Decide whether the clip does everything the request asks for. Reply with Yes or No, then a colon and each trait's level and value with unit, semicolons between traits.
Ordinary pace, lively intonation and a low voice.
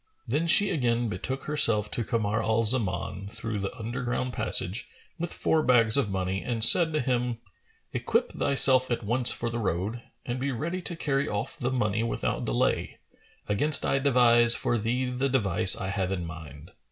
No: average, 175 wpm; average, 4.0 semitones; low, 120 Hz